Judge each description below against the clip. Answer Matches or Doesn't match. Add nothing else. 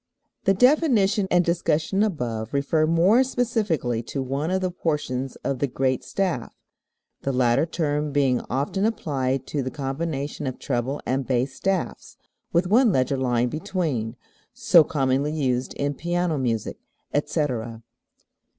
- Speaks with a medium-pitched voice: Matches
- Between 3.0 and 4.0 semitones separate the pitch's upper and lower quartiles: Doesn't match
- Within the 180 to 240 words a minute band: Doesn't match